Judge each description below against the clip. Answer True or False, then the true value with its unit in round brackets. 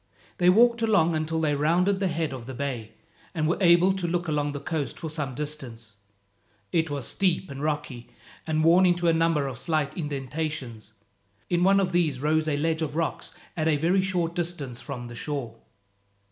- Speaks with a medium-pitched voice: True (155 Hz)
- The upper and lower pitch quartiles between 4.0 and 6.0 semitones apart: False (3.5 semitones)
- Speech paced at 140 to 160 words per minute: False (190 wpm)